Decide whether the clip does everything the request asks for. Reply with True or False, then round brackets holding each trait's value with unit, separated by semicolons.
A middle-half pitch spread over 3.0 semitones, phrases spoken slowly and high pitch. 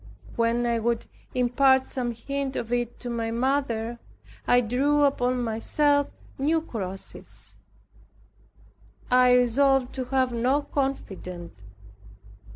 False (2.6 semitones; 110 wpm; 245 Hz)